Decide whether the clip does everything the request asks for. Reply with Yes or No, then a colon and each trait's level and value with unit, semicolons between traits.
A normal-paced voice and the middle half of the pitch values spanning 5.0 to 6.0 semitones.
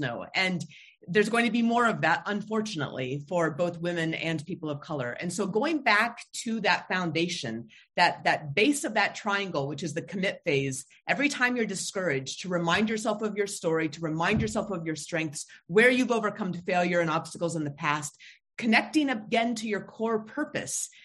Yes: average, 190 wpm; average, 5.3 semitones